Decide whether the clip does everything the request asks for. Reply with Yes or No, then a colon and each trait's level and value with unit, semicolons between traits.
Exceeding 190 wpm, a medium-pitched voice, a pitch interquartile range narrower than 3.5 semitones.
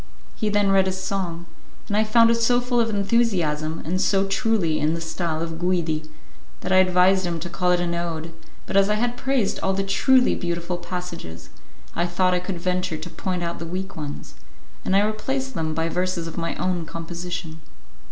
Yes: average, 200 wpm; medium, 180 Hz; average, 3.0 semitones